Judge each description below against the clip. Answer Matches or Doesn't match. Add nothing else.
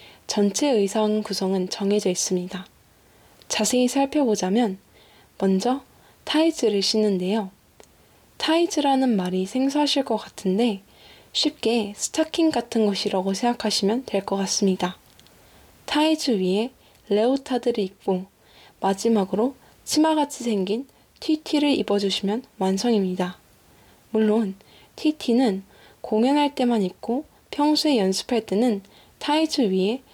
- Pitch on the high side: Matches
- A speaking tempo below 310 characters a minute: Matches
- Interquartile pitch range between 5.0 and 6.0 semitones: Matches